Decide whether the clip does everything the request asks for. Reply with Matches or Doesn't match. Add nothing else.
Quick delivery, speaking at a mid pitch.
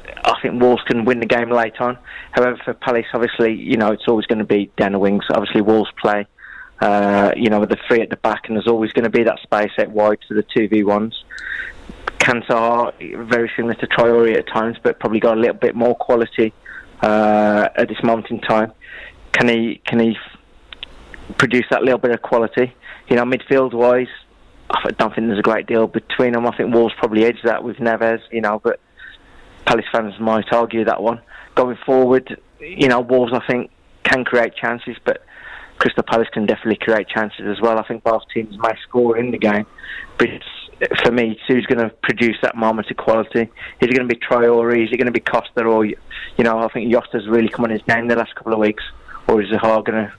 Doesn't match